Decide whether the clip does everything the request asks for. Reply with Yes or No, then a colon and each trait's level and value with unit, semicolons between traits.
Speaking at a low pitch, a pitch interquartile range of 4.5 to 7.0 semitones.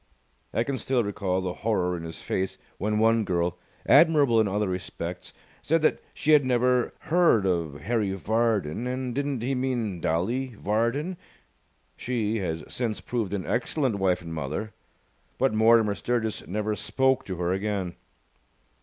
Yes: low, 110 Hz; average, 5.2 semitones